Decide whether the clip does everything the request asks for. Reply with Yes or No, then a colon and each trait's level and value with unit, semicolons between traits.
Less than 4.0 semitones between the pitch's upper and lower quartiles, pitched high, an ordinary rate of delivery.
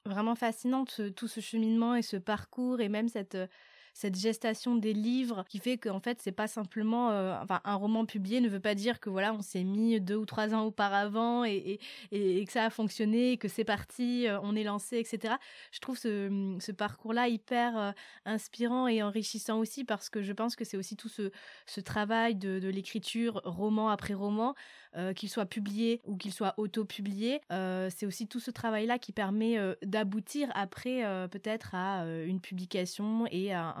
Yes: narrow, 2.4 semitones; high, 215 Hz; average, 205 wpm